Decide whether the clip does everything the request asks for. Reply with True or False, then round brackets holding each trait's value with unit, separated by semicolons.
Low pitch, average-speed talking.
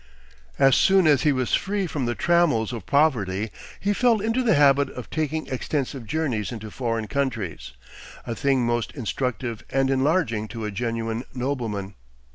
True (130 Hz; 160 wpm)